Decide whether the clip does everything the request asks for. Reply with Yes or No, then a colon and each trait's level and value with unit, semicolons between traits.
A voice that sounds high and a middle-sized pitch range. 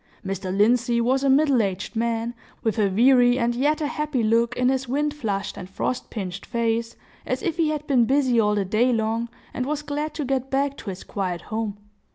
Yes: high, 240 Hz; average, 3.8 semitones